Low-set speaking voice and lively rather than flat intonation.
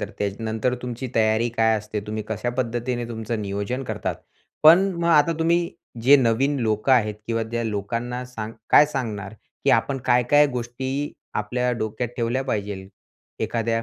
No: low, 115 Hz; average, 2.8 semitones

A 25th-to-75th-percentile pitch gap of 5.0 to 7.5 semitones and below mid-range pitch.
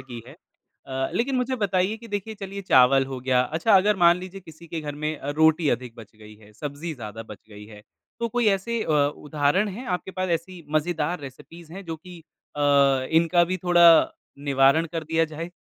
No: wide, 5.5 semitones; medium, 165 Hz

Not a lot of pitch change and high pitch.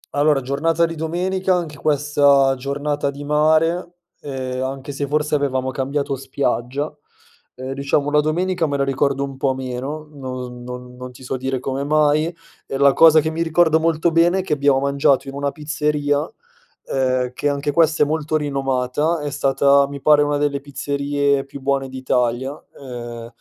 No: narrow, 2.2 semitones; medium, 140 Hz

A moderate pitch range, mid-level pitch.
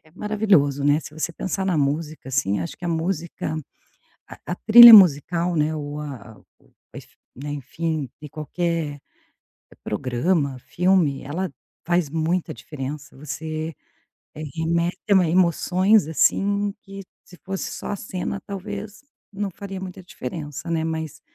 Yes: average, 4.3 semitones; medium, 165 Hz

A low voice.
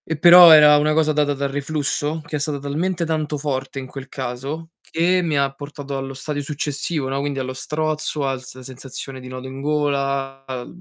No: medium, 145 Hz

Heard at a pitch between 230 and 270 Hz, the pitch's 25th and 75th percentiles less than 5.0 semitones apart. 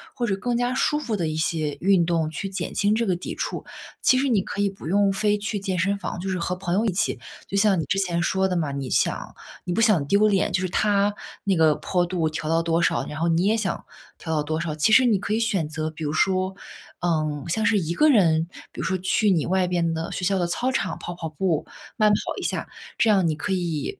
No: medium, 185 Hz; average, 3.7 semitones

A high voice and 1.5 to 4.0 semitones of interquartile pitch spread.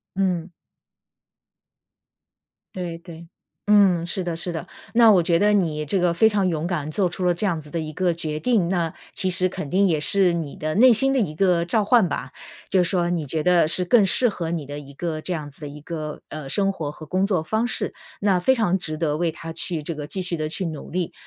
No: medium, 175 Hz; average, 3.4 semitones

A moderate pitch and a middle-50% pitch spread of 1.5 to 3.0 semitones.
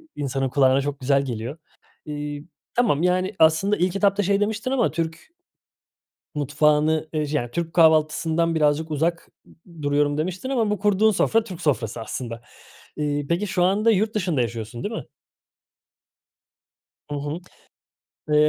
No: medium, 155 Hz; average, 4.5 semitones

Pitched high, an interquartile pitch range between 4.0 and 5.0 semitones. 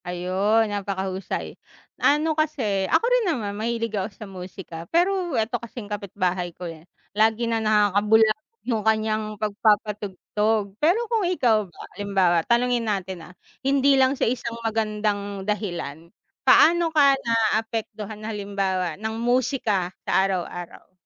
No: high, 215 Hz; average, 3.4 semitones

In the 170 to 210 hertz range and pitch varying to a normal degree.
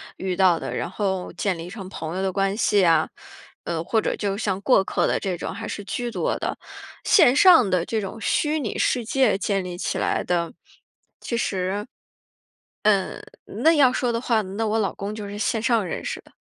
Yes: high, 200 Hz; average, 3.6 semitones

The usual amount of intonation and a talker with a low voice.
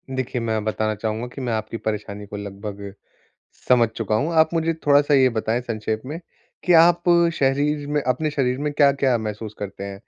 Yes: average, 4.8 semitones; low, 120 Hz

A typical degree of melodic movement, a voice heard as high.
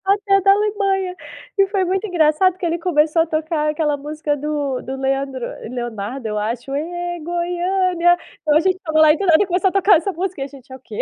Yes: average, 4.4 semitones; very high, 330 Hz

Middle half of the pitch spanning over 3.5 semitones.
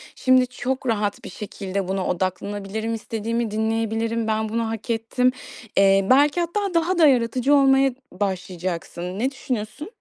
Yes: average, 4.2 semitones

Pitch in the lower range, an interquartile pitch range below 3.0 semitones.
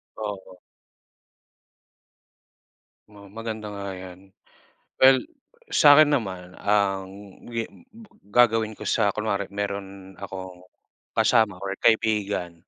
Yes: low, 100 Hz; narrow, 2.4 semitones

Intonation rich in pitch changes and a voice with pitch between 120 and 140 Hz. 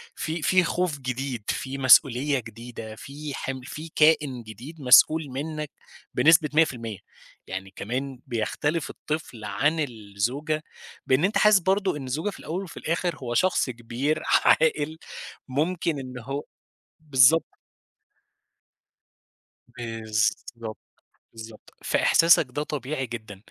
No: average, 4.8 semitones; low, 135 Hz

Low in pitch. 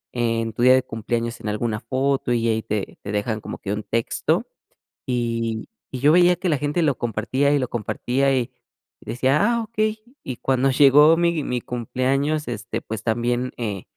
Yes: low, 125 Hz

